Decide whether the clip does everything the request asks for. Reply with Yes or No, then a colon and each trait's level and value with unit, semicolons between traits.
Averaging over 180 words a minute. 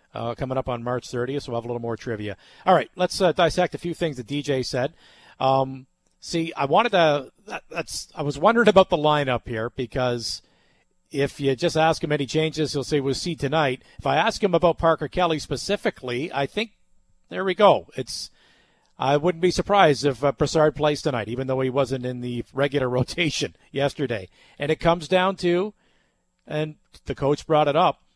Yes: average, 200 wpm